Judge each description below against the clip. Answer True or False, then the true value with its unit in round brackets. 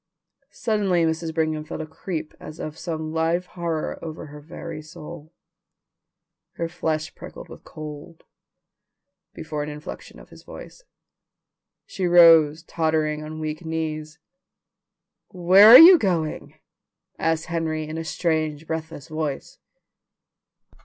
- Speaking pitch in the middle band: True (160 Hz)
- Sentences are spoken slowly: True (125 wpm)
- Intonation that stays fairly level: True (1.5 semitones)